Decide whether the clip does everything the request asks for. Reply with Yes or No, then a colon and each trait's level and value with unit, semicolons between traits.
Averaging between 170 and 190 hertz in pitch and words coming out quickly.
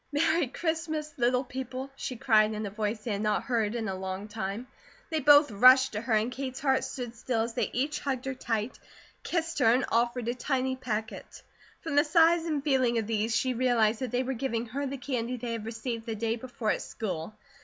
No: high, 245 Hz; fast, 220 wpm